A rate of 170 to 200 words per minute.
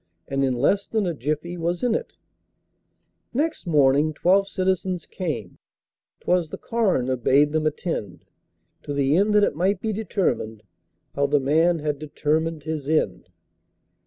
No: average, 150 wpm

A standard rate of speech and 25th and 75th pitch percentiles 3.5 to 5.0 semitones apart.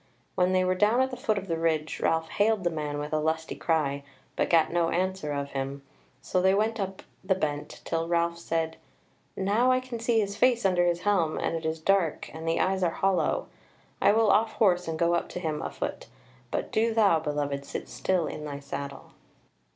No: fast, 215 wpm; average, 3.9 semitones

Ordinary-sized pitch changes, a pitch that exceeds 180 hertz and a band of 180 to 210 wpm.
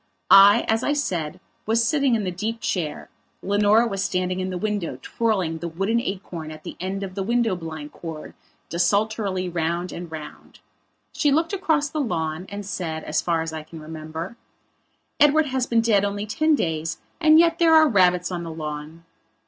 No: wide, 5.7 semitones; high, 190 Hz; average, 185 wpm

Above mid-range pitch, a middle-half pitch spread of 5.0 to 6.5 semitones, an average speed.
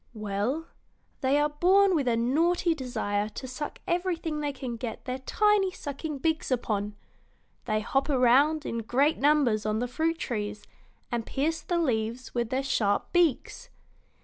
Yes: very high, 270 Hz; wide, 5.4 semitones; average, 155 wpm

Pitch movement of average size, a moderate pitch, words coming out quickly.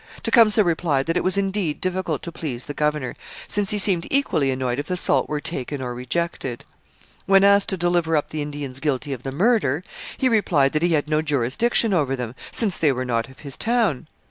No: wide, 5.9 semitones; medium, 155 Hz; fast, 210 wpm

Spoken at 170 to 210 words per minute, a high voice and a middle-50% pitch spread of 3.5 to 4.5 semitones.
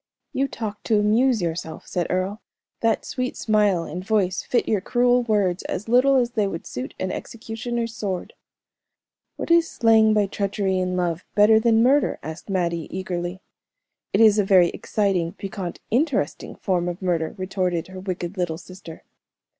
No: average, 160 wpm; high, 195 Hz; average, 3.8 semitones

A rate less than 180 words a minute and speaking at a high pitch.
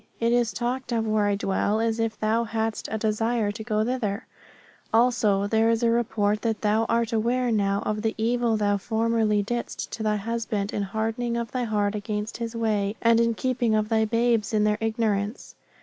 No: average, 195 wpm; high, 220 Hz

